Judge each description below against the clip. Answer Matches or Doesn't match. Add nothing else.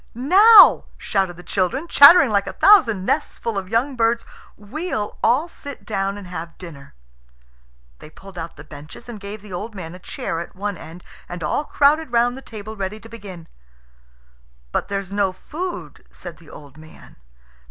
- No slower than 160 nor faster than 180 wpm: Matches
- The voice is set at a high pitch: Matches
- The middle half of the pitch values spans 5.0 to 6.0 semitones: Matches